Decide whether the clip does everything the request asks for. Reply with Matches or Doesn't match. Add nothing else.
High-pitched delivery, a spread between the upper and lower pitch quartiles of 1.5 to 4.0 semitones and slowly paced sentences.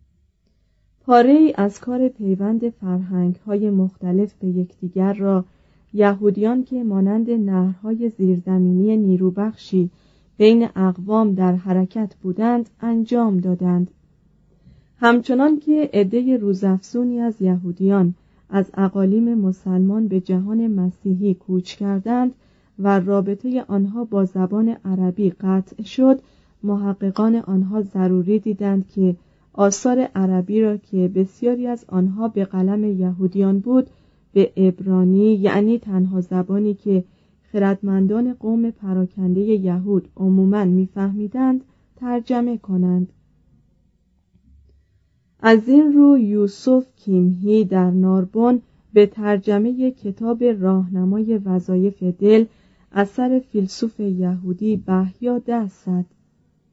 Matches